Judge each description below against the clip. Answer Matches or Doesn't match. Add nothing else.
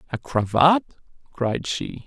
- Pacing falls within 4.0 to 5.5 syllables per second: Doesn't match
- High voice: Doesn't match